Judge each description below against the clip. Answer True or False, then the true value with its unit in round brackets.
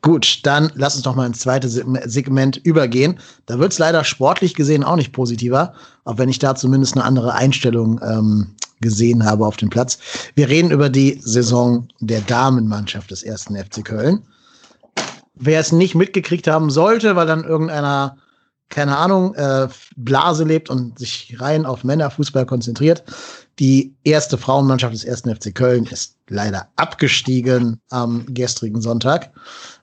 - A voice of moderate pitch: False (130 Hz)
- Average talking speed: True (155 wpm)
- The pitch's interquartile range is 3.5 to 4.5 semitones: True (4.1 semitones)